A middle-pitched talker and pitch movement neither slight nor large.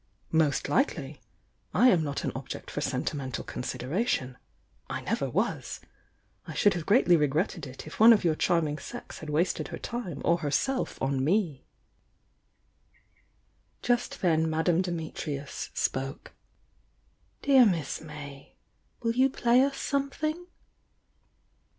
No: medium, 165 Hz; wide, 8.0 semitones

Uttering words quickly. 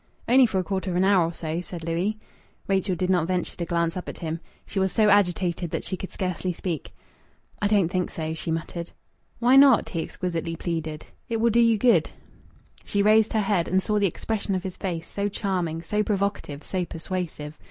Yes: fast, 210 wpm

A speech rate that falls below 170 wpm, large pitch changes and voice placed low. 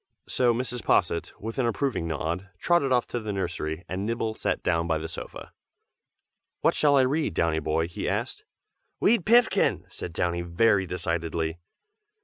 Yes: average, 160 wpm; wide, 6.8 semitones; very low, 95 Hz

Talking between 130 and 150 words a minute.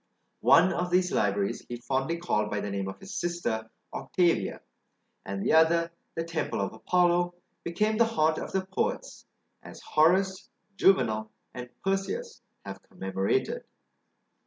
Yes: average, 140 wpm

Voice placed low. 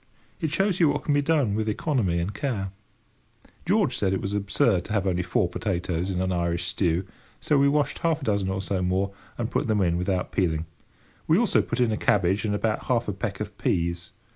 Yes: low, 100 Hz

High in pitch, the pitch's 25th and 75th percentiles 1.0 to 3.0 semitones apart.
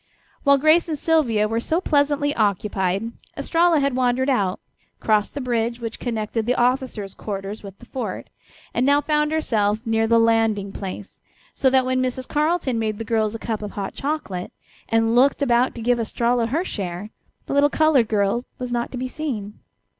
No: high, 235 Hz; average, 4.6 semitones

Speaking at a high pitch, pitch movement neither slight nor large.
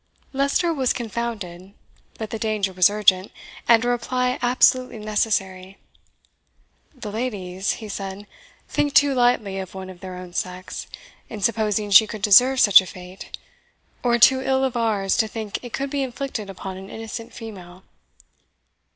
Yes: high, 215 Hz; average, 4.2 semitones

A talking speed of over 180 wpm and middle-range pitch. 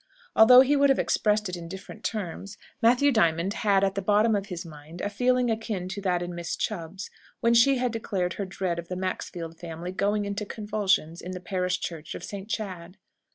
No: average, 200 wpm; high, 195 Hz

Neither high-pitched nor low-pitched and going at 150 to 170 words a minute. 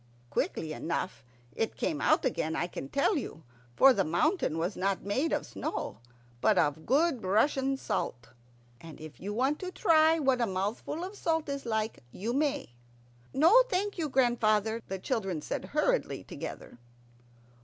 No: high, 235 Hz; average, 160 wpm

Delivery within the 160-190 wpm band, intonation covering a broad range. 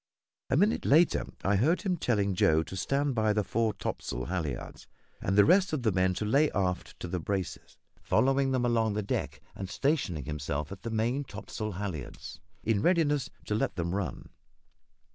Yes: average, 180 wpm; wide, 6.7 semitones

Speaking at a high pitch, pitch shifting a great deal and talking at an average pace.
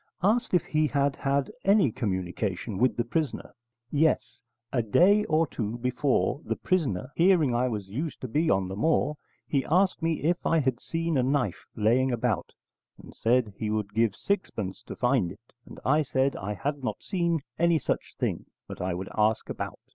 No: low, 130 Hz; wide, 6.8 semitones; average, 185 wpm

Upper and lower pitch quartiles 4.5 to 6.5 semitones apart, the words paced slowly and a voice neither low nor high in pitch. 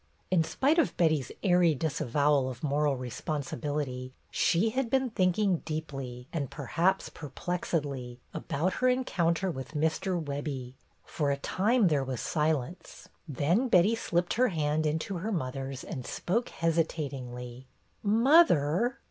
Yes: average, 5.1 semitones; slow, 130 wpm; medium, 155 Hz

